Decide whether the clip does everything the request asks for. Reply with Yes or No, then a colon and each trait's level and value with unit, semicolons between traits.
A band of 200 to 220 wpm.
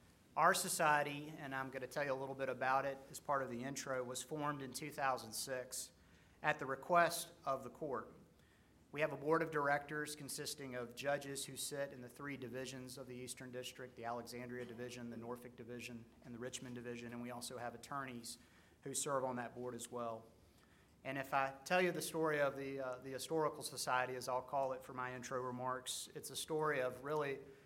Yes: fast, 205 wpm